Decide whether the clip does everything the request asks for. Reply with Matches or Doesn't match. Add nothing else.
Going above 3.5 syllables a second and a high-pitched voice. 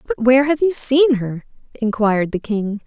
Matches